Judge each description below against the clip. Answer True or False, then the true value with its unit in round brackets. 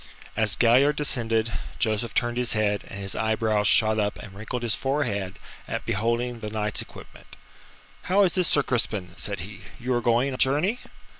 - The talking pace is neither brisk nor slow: True (175 wpm)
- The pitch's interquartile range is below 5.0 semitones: True (3.1 semitones)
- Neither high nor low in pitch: False (115 Hz)